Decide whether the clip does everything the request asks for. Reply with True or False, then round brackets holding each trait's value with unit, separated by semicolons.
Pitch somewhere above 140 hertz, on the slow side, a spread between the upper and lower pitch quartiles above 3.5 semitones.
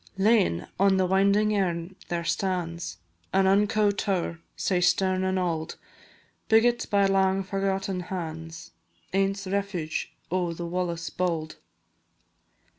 False (190 Hz; 115 wpm; 2.4 semitones)